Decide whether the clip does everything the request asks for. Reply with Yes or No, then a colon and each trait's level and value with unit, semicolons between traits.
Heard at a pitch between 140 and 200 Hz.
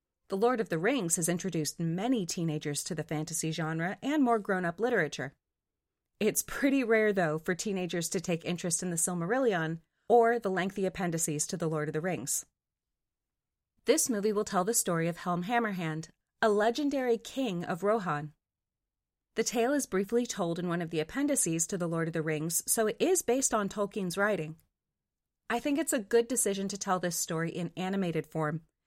Yes: medium, 185 Hz